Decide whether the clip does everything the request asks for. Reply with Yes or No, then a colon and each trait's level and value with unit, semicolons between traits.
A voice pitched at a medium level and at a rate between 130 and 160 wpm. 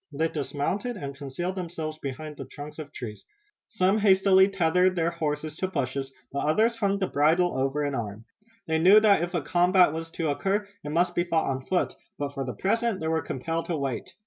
No: medium, 160 Hz; fast, 205 wpm